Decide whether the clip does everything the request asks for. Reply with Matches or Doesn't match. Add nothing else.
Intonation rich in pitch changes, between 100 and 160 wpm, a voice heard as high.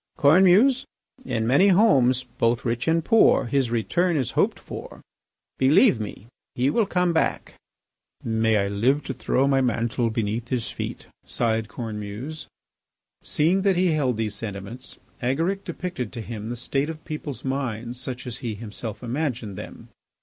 Doesn't match